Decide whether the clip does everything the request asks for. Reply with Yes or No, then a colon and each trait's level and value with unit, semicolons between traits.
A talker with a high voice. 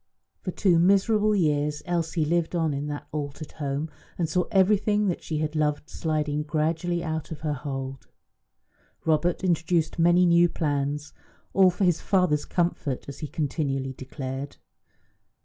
No: medium, 160 Hz